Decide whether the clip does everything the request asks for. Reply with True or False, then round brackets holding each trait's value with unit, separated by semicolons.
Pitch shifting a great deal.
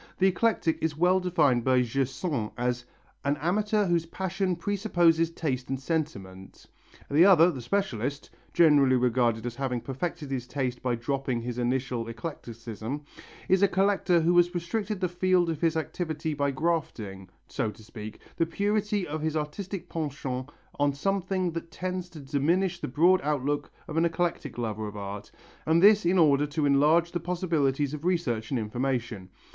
True (5.7 semitones)